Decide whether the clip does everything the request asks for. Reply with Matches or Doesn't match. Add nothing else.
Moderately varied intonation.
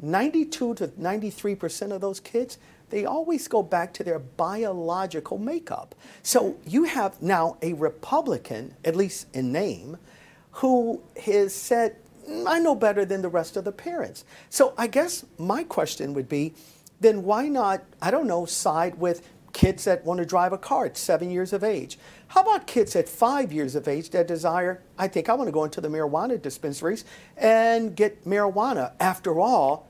Doesn't match